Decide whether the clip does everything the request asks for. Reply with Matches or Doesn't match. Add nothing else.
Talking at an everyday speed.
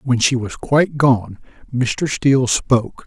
Matches